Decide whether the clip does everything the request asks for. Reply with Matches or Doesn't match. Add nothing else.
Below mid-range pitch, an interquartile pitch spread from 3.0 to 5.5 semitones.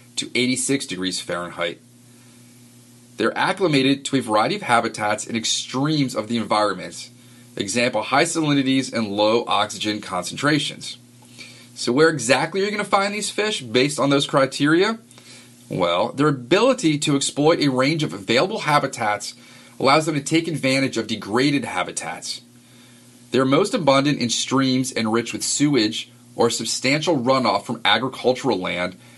Matches